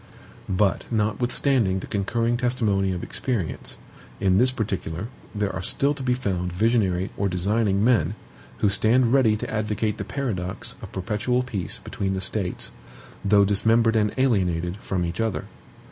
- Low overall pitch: Yes, low, 105 Hz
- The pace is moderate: Yes, average, 150 wpm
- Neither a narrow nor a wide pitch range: Yes, average, 3.5 semitones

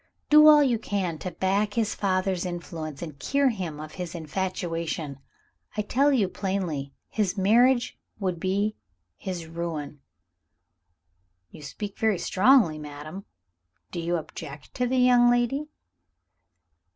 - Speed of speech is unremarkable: No, slow, 130 wpm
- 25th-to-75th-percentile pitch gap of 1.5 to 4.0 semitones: No, average, 5.2 semitones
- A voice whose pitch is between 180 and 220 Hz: Yes, high, 190 Hz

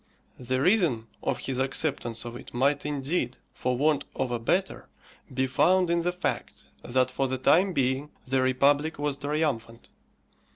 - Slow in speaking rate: No, average, 160 wpm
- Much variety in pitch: No, average, 3.3 semitones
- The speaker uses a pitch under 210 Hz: Yes, low, 135 Hz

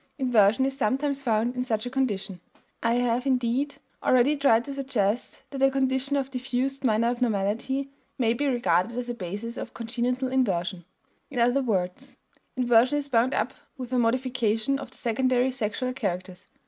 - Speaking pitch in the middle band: No, high, 245 Hz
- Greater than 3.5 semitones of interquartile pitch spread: No, average, 2.9 semitones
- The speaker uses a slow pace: No, average, 165 wpm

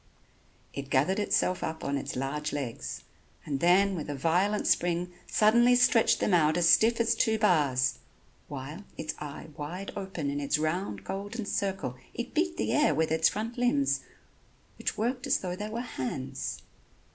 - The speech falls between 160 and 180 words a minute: Yes, average, 170 wpm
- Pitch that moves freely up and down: Yes, wide, 6.8 semitones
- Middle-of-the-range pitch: Yes, medium, 180 Hz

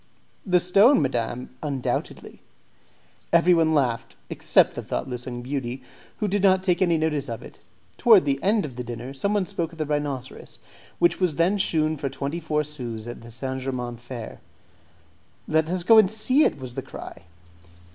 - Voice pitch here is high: No, medium, 150 Hz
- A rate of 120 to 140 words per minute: No, average, 175 wpm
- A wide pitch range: Yes, wide, 6.0 semitones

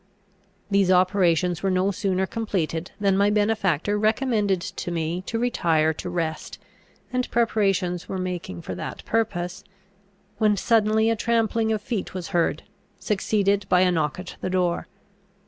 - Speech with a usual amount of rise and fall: Yes, average, 3.3 semitones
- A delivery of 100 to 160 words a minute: Yes, average, 145 wpm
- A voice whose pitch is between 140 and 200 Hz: Yes, high, 190 Hz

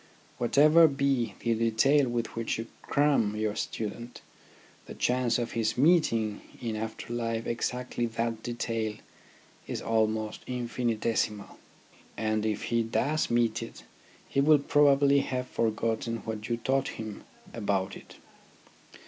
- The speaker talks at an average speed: No, slow, 130 wpm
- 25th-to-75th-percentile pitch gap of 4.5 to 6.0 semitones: No, narrow, 2.4 semitones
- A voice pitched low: Yes, low, 115 Hz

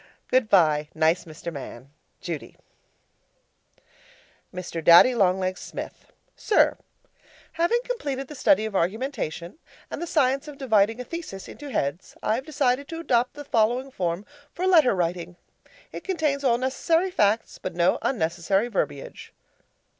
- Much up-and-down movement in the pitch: Yes, wide, 8.1 semitones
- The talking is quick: No, average, 140 wpm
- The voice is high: Yes, high, 230 Hz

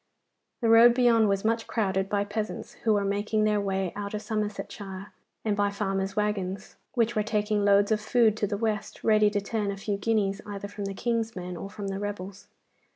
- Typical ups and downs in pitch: No, narrow, 1.6 semitones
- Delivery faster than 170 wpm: Yes, fast, 205 wpm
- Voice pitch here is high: Yes, high, 205 Hz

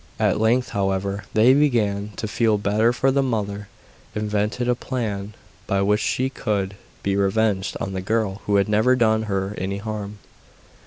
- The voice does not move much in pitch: Yes, narrow, 2.2 semitones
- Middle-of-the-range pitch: No, low, 105 Hz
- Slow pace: No, average, 165 wpm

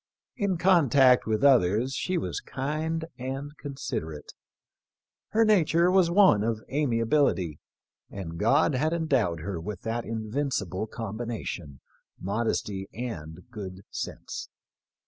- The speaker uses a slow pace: Yes, slow, 115 wpm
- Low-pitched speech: Yes, low, 120 Hz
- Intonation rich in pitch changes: Yes, wide, 7.2 semitones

